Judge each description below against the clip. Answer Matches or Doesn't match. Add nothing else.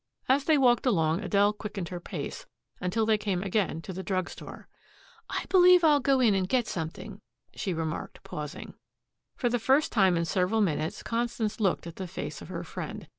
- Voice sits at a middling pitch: Doesn't match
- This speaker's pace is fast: Doesn't match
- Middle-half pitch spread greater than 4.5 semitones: Matches